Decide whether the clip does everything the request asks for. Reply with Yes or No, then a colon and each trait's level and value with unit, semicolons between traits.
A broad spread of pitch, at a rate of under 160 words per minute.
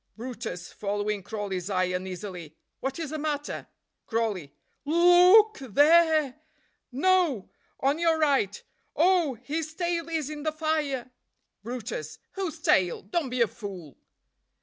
Yes: wide, 7.6 semitones; average, 150 wpm